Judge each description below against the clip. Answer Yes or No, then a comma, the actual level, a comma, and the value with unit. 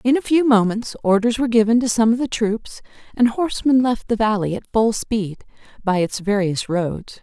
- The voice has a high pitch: Yes, high, 220 Hz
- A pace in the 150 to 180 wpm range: No, average, 200 wpm